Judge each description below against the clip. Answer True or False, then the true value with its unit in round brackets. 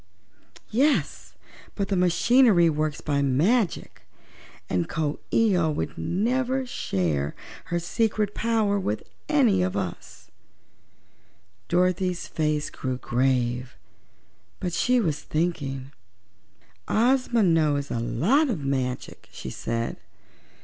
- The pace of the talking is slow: True (110 wpm)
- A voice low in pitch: False (170 Hz)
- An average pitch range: False (8.1 semitones)